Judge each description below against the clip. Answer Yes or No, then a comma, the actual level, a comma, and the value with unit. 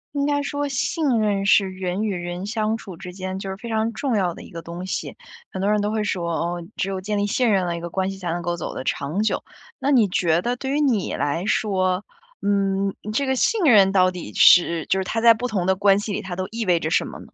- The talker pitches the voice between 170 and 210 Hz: Yes, high, 195 Hz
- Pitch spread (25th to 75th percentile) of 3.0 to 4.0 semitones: Yes, average, 3.4 semitones